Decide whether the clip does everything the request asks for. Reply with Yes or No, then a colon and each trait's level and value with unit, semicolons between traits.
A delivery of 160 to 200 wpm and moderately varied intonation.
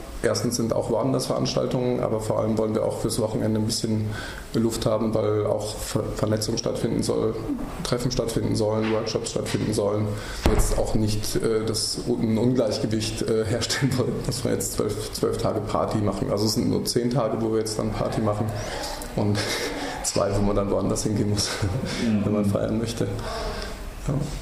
No: average, 170 wpm; narrow, 1.4 semitones